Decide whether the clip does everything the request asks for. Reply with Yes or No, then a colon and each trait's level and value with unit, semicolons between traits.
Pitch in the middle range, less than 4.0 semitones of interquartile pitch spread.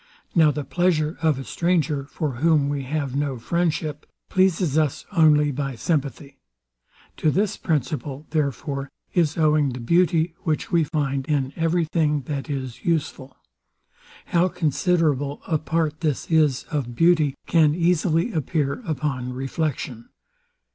Yes: medium, 150 Hz; average, 3.0 semitones